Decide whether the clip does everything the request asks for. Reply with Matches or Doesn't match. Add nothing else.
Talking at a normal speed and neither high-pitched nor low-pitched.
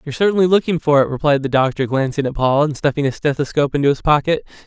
Doesn't match